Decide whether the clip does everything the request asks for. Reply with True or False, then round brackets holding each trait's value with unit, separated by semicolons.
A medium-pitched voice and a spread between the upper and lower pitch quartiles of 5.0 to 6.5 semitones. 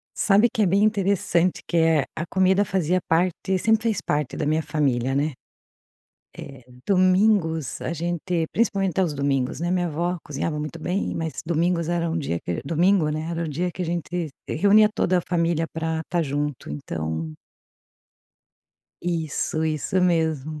False (165 Hz; 3.3 semitones)